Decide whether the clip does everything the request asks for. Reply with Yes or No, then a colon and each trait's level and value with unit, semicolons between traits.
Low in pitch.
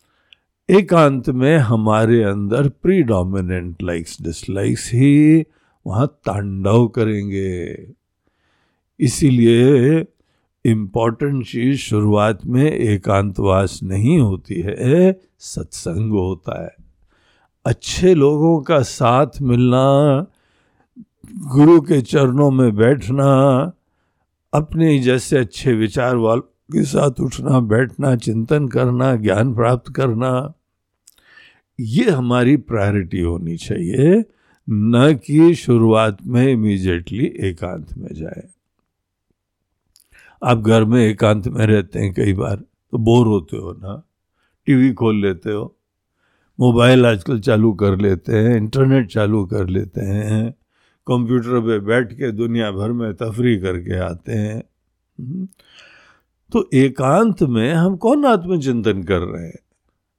Yes: low, 115 Hz